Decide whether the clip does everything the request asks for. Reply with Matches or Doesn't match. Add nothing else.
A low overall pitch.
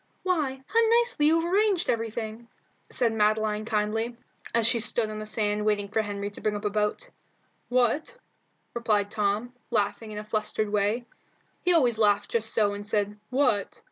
Doesn't match